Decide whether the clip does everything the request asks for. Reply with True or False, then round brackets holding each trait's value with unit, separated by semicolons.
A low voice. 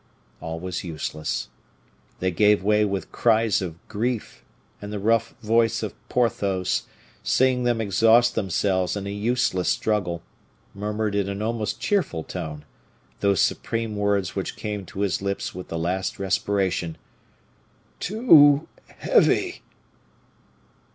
True (100 Hz)